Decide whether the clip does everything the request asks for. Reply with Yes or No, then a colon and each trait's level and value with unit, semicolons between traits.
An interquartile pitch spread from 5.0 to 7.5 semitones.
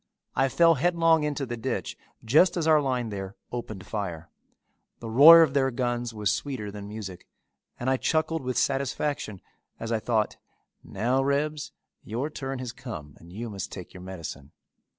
Yes: wide, 5.5 semitones